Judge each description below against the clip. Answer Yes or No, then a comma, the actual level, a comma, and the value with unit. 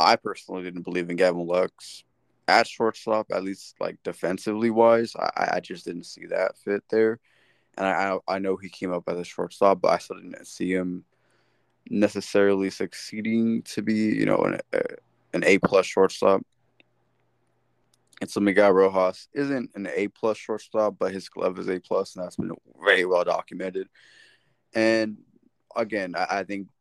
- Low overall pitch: Yes, low, 100 Hz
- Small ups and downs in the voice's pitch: No, average, 3.0 semitones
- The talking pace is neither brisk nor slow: Yes, average, 170 wpm